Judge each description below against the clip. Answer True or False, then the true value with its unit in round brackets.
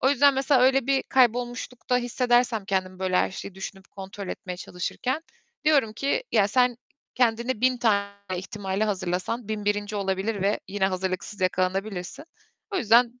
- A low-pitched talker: False (215 Hz)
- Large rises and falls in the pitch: False (4.5 semitones)